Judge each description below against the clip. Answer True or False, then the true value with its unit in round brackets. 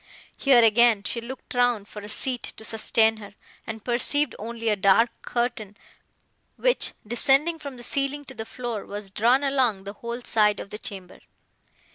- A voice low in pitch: False (235 Hz)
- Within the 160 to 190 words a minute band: True (170 wpm)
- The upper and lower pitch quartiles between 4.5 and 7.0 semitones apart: False (3.3 semitones)